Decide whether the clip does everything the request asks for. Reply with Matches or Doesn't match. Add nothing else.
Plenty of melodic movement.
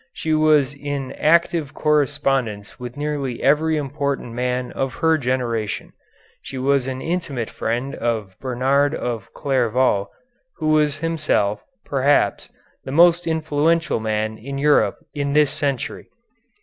Doesn't match